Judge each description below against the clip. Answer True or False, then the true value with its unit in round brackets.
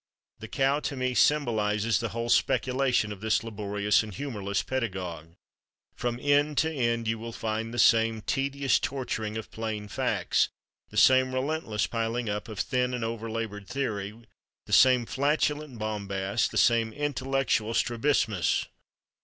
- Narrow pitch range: False (3.5 semitones)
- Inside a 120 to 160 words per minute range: True (145 wpm)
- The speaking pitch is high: False (115 Hz)